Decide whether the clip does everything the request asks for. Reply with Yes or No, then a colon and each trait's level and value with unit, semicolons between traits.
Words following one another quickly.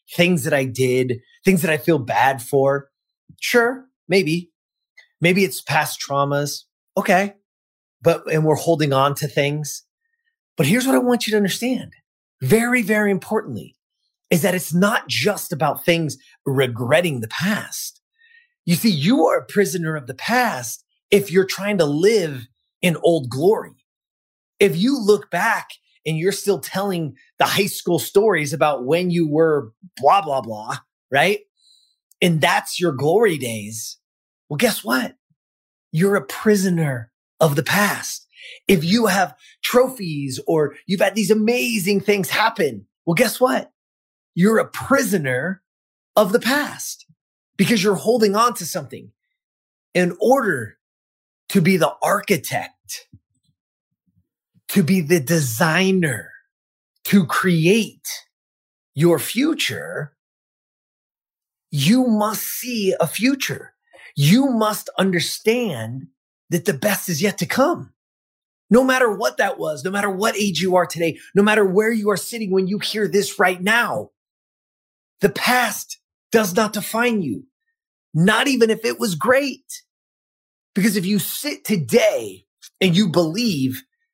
No: average, 140 wpm